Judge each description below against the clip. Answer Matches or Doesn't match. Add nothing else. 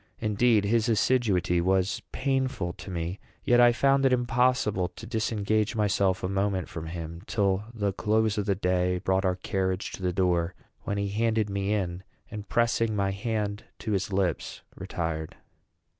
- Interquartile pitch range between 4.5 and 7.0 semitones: Doesn't match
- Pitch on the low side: Matches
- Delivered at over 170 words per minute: Doesn't match